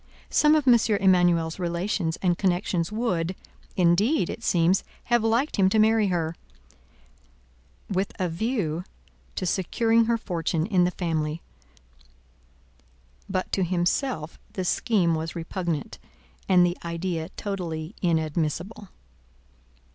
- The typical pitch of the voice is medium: Yes, medium, 180 Hz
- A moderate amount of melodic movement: Yes, average, 3.8 semitones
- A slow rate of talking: Yes, slow, 115 wpm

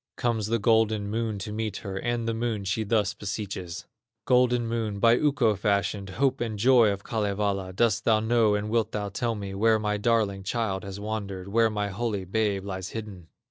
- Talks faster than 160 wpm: Yes, average, 190 wpm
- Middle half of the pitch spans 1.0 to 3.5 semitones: Yes, narrow, 2.5 semitones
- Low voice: Yes, low, 105 Hz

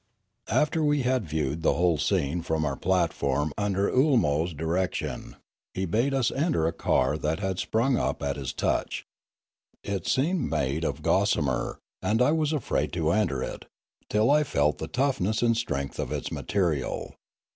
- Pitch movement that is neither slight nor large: No, wide, 8.5 semitones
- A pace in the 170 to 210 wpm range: Yes, average, 175 wpm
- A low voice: Yes, very low, 90 Hz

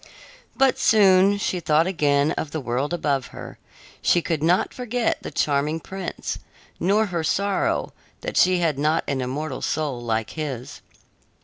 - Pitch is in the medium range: Yes, medium, 160 Hz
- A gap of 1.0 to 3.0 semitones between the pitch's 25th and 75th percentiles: No, average, 4.7 semitones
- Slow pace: No, average, 150 wpm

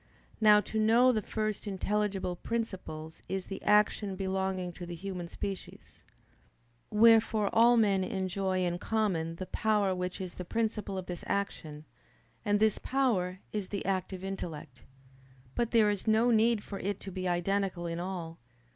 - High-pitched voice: Yes, high, 195 Hz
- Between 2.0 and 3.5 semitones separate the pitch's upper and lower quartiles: Yes, average, 2.9 semitones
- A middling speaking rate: Yes, average, 155 wpm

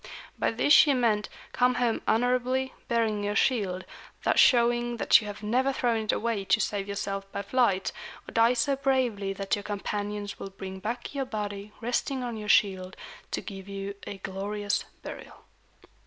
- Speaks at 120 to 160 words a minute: No, average, 170 wpm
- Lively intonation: No, average, 3.5 semitones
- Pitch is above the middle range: Yes, high, 215 Hz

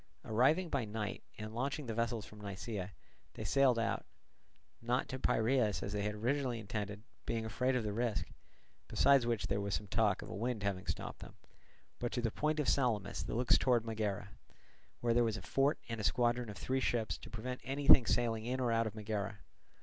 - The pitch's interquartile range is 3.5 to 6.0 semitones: No, average, 3.1 semitones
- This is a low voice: Yes, low, 115 Hz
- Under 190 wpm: No, average, 200 wpm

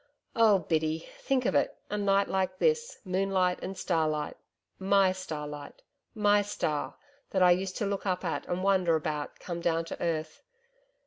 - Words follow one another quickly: No, average, 165 wpm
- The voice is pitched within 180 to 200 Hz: Yes, medium, 185 Hz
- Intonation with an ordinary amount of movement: Yes, average, 3.3 semitones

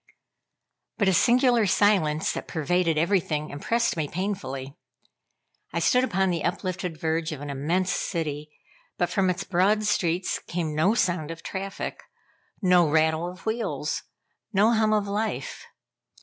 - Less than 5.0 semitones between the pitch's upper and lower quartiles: Yes, average, 4.2 semitones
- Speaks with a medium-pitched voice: Yes, medium, 180 Hz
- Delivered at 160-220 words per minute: No, average, 140 wpm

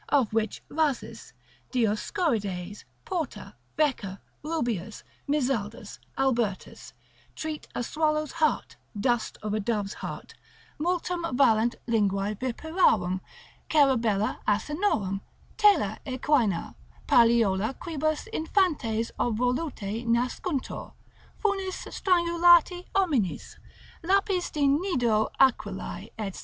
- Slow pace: Yes, slow, 90 wpm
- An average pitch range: No, wide, 6.9 semitones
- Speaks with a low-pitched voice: No, very high, 250 Hz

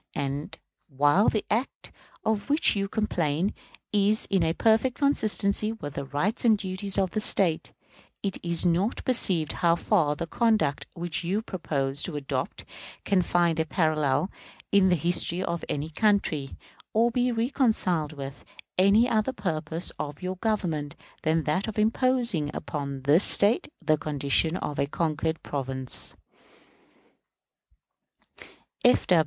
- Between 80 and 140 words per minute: Yes, slow, 135 wpm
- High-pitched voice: No, medium, 175 Hz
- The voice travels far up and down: Yes, wide, 6.0 semitones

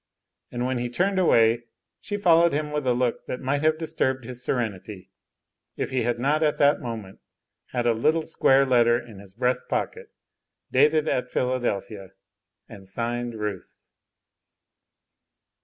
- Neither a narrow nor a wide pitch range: Yes, average, 4.0 semitones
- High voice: No, low, 125 Hz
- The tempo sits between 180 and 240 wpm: No, average, 150 wpm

